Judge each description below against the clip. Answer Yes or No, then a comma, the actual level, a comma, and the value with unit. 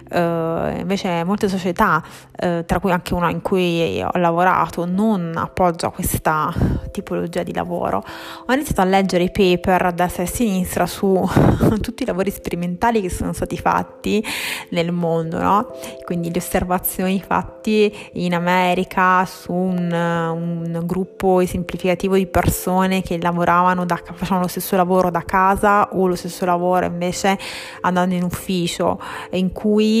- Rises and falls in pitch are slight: Yes, narrow, 1.7 semitones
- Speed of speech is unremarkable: Yes, average, 145 wpm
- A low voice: No, medium, 180 Hz